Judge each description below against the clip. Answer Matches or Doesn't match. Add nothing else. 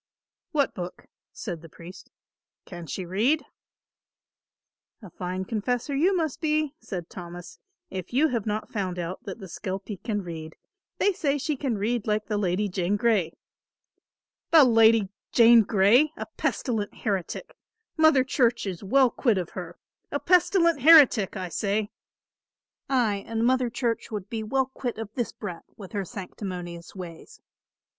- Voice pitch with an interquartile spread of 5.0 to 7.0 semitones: Matches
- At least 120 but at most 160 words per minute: Matches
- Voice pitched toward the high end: Matches